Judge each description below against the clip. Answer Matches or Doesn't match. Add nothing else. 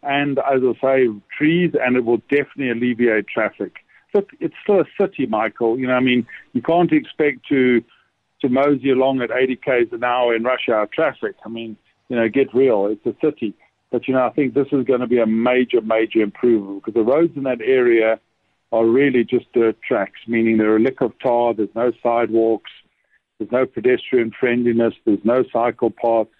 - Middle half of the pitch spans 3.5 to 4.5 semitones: Doesn't match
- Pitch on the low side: Matches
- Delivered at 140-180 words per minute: Doesn't match